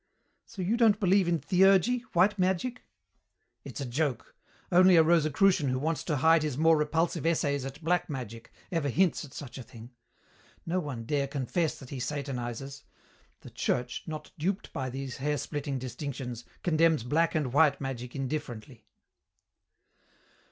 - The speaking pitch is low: No, medium, 150 Hz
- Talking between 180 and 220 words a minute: No, average, 155 wpm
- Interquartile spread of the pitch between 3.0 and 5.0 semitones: Yes, average, 4.4 semitones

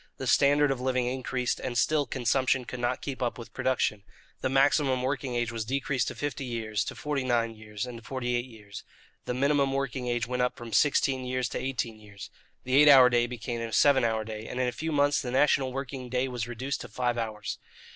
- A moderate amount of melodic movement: No, narrow, 2.3 semitones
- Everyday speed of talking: No, fast, 225 wpm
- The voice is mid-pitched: No, low, 125 Hz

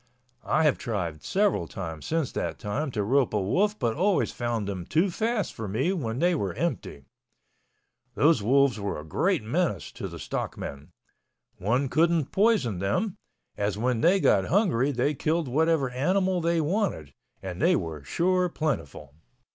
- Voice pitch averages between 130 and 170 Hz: Yes, low, 135 Hz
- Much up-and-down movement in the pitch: Yes, wide, 9.0 semitones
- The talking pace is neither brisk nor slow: Yes, average, 165 wpm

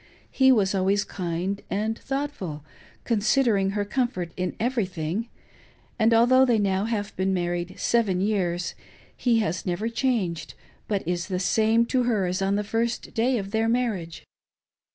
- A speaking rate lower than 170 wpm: Yes, average, 155 wpm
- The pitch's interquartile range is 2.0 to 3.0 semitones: No, average, 4.1 semitones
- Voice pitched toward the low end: No, high, 205 Hz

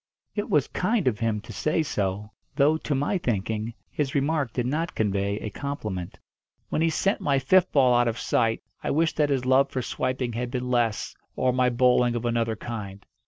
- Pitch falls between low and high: No, low, 125 Hz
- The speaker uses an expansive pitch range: No, average, 4.1 semitones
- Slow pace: No, average, 200 wpm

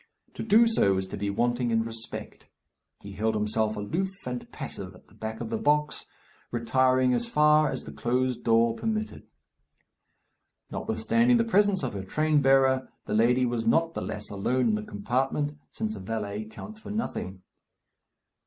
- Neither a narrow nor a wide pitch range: No, wide, 6.1 semitones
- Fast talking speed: No, average, 170 wpm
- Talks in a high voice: No, low, 125 Hz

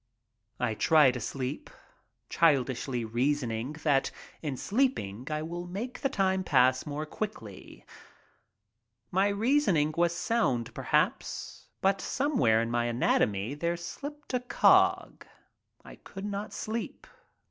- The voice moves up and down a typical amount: No, wide, 8.0 semitones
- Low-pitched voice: No, medium, 155 Hz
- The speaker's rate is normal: No, slow, 120 wpm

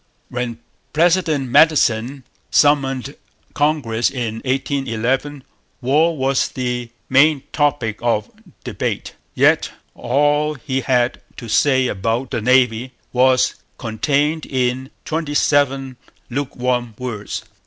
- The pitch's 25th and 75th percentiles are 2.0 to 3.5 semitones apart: Yes, average, 3.0 semitones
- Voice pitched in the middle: No, low, 130 Hz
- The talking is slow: Yes, slow, 100 wpm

